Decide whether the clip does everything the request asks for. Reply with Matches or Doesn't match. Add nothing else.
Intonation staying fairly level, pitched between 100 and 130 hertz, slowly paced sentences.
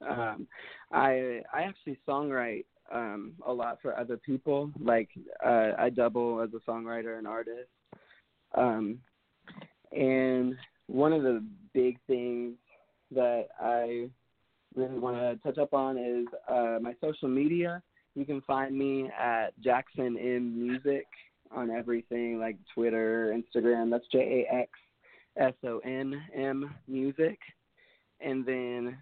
Matches